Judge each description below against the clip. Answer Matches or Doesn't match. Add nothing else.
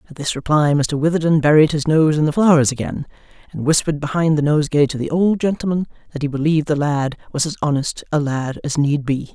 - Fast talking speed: Matches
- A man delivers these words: Doesn't match